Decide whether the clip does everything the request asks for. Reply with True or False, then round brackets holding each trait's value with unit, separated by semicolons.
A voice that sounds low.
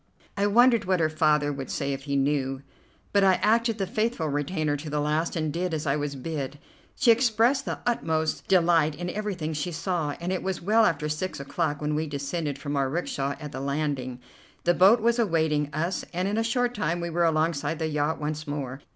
False (160 Hz)